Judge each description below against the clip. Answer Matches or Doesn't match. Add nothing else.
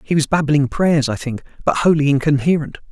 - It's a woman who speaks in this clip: Doesn't match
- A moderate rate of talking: Matches